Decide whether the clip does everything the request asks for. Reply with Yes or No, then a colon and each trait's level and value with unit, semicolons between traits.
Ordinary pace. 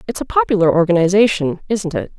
Yes: average, 165 wpm